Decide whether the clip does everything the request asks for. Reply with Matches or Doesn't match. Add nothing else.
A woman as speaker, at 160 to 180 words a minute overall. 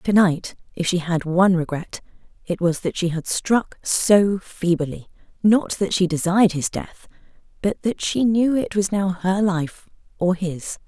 Matches